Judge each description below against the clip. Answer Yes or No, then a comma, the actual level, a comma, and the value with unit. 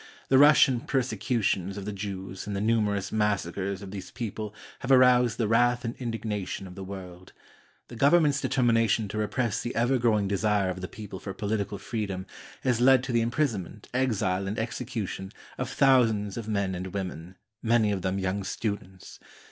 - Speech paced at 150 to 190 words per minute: Yes, average, 180 wpm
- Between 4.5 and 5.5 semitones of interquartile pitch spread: No, average, 3.7 semitones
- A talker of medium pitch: No, low, 105 Hz